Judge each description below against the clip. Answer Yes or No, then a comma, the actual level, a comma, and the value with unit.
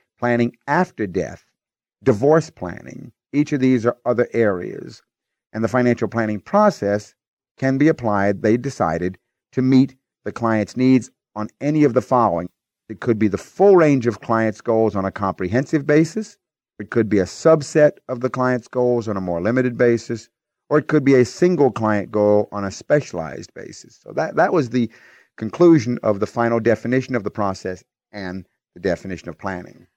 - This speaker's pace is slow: No, average, 175 wpm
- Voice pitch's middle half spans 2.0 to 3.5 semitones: No, average, 4.3 semitones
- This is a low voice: Yes, low, 120 Hz